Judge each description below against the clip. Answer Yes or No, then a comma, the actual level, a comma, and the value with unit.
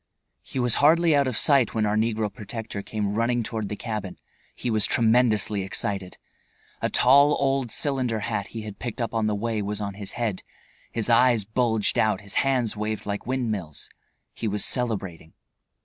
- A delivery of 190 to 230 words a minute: No, average, 180 wpm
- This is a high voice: No, low, 110 Hz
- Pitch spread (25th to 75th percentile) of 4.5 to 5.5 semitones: No, average, 3.0 semitones